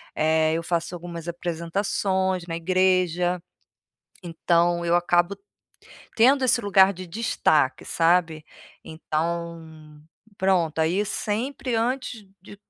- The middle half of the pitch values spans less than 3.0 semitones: Yes, narrow, 2.6 semitones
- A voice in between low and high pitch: Yes, medium, 175 Hz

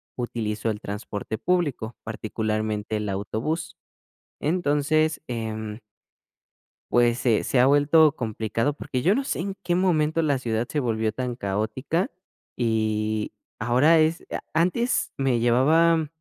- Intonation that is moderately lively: No, wide, 6.2 semitones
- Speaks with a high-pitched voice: No, low, 125 Hz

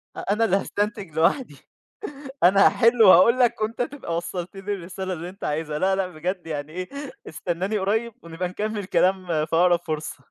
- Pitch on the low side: No, medium, 185 Hz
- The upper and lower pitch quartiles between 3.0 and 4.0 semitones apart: Yes, average, 3.4 semitones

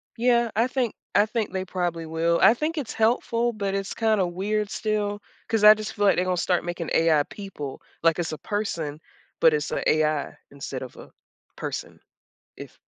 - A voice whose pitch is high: Yes, high, 195 Hz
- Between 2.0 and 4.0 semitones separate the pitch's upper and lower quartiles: No, average, 4.8 semitones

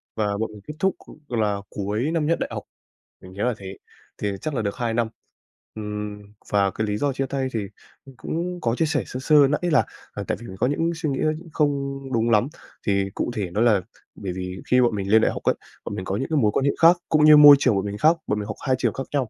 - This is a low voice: Yes, low, 115 Hz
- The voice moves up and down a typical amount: No, wide, 5.9 semitones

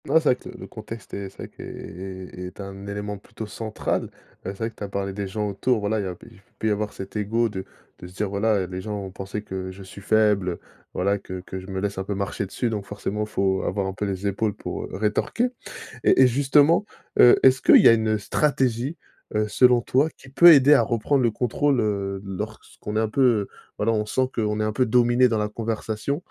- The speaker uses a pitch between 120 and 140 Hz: No, low, 105 Hz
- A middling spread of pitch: Yes, average, 3.0 semitones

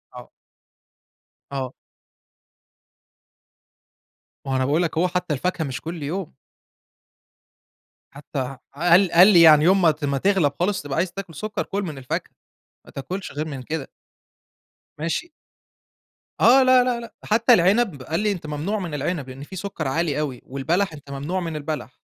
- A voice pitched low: No, medium, 165 Hz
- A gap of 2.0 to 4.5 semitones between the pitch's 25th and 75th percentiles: No, average, 5.0 semitones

